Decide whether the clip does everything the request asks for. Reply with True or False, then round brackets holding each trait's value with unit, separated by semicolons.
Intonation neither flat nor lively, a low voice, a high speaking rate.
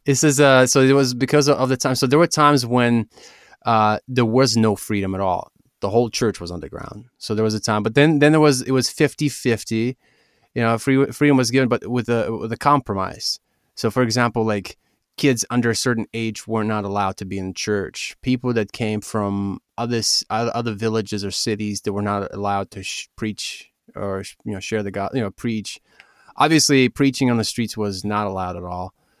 True (4.0 semitones; 115 Hz; 215 wpm)